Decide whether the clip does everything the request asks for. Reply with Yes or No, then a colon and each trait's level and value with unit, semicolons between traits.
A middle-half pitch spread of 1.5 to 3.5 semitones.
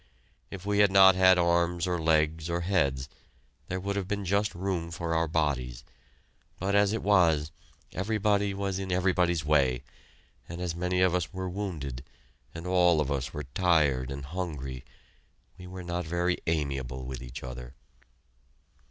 No: average, 4.2 semitones